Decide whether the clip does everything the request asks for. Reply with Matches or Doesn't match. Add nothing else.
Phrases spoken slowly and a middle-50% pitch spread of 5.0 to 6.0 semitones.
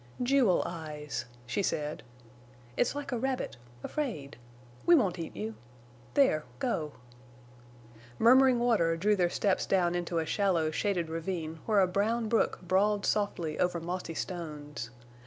Matches